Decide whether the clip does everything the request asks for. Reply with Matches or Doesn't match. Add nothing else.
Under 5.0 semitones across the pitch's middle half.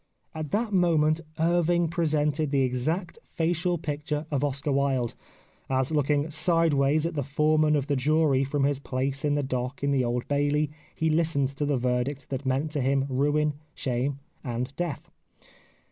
Matches